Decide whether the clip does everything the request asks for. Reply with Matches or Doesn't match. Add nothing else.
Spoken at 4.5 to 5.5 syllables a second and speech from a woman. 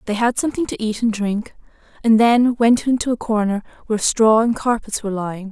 Doesn't match